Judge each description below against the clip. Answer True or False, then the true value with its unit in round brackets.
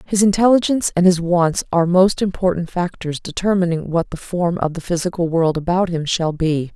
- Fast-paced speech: False (185 wpm)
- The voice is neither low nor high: True (175 Hz)